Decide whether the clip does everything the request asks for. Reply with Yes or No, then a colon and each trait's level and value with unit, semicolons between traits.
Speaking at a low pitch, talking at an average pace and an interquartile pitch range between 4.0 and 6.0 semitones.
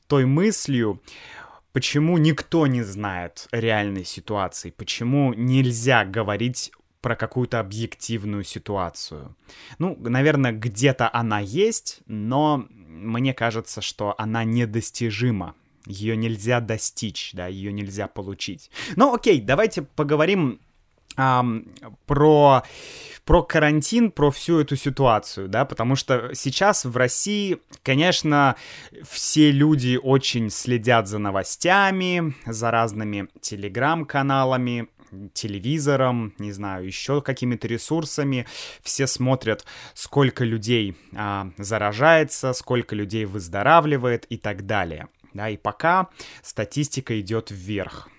No: low, 120 Hz; slow, 105 wpm; average, 5.1 semitones